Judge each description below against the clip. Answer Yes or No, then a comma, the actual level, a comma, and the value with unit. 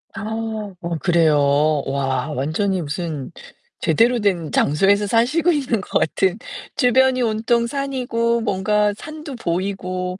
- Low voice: No, high, 200 Hz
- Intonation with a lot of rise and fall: Yes, wide, 5.8 semitones